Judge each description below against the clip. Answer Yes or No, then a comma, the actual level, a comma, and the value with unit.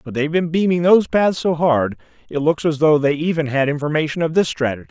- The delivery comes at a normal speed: No, fast, 235 wpm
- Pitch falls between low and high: Yes, medium, 155 Hz